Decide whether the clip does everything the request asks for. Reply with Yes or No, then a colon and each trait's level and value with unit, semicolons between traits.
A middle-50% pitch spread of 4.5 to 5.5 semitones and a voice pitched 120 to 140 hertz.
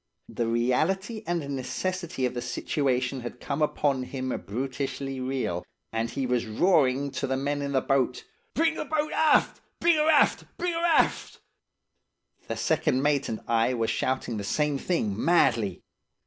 Yes: average, 5.1 semitones; low, 135 Hz